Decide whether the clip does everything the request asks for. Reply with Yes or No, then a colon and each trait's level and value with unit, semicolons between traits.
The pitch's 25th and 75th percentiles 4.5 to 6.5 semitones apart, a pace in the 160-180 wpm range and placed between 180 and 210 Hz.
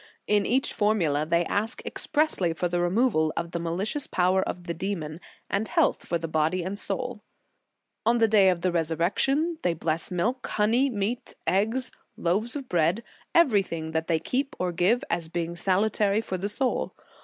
Yes: average, 5.2 semitones; average, 175 wpm; high, 190 Hz